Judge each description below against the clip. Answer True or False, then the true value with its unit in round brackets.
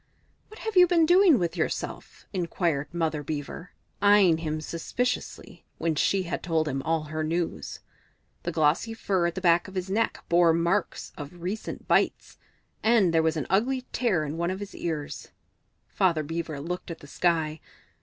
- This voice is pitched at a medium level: True (170 Hz)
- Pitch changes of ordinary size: True (3.7 semitones)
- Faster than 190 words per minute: False (175 wpm)